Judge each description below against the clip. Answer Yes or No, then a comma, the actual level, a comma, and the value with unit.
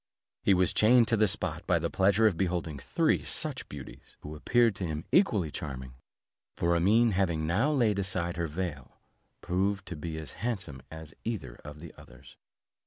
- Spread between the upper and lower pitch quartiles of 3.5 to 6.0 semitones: Yes, average, 4.5 semitones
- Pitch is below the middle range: Yes, very low, 90 Hz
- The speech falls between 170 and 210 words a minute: Yes, average, 175 wpm